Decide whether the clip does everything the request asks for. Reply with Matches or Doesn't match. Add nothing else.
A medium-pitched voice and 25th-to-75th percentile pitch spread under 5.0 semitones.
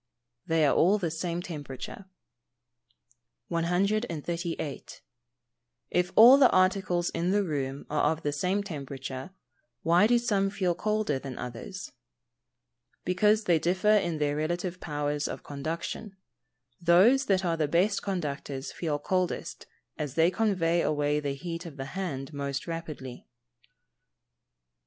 Matches